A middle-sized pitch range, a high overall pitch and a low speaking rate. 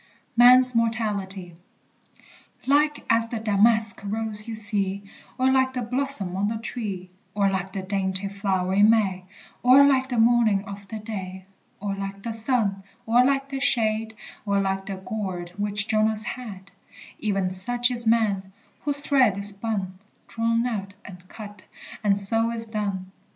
No: average, 3.0 semitones; high, 210 Hz; average, 155 wpm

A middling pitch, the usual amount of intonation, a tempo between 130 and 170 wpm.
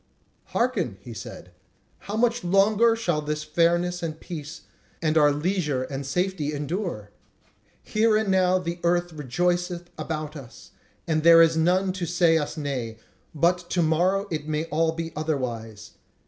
Yes: medium, 165 Hz; average, 3.1 semitones; average, 150 wpm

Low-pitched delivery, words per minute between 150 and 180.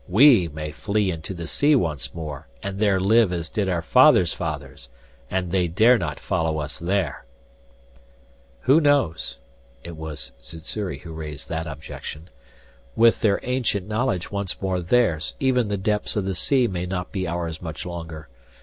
Yes: very low, 90 Hz; average, 170 wpm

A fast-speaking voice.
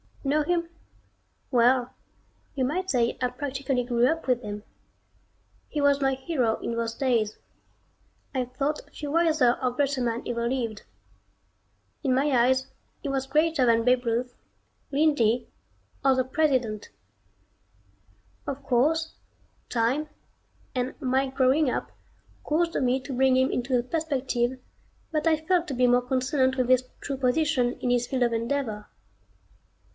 No: average, 145 wpm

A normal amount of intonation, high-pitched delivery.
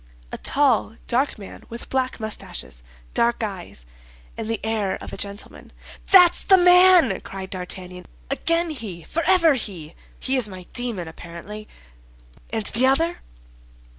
No: wide, 6.9 semitones; high, 225 Hz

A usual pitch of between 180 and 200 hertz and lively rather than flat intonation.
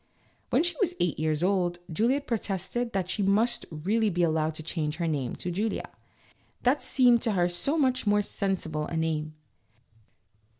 Yes: high, 190 Hz; wide, 6.2 semitones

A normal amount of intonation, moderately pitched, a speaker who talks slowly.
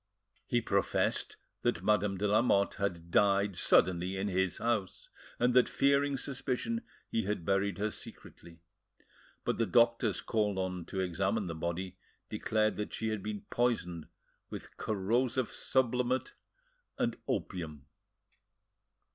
No: average, 4.0 semitones; low, 100 Hz; slow, 130 wpm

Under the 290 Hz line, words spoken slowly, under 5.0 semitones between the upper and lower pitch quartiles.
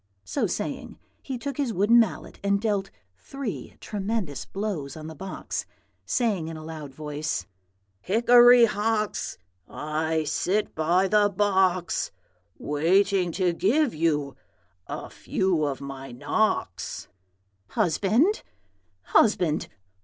No: high, 190 Hz; slow, 115 wpm; wide, 5.5 semitones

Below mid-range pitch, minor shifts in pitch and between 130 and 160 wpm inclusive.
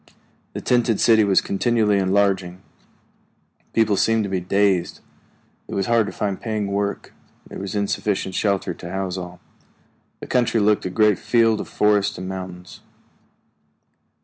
Yes: low, 100 Hz; narrow, 2.3 semitones; average, 150 wpm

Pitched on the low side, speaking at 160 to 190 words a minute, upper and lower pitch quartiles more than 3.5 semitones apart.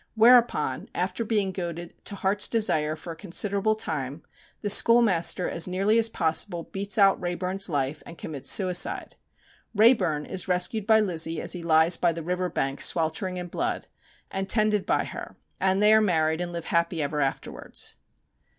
No: medium, 180 Hz; average, 170 wpm; average, 4.0 semitones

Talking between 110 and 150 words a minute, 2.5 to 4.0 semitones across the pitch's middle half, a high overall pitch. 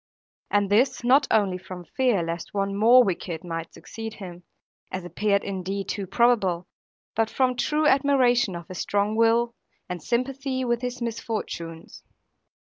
No: average, 145 wpm; average, 4.9 semitones; high, 215 Hz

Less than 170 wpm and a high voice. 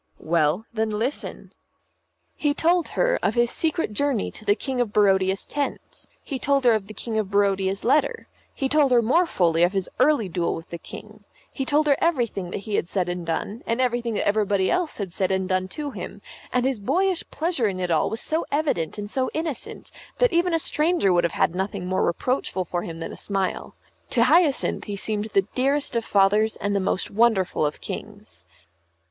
No: fast, 205 wpm; high, 215 Hz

